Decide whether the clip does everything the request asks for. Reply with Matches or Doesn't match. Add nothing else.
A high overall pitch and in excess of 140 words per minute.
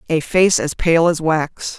Doesn't match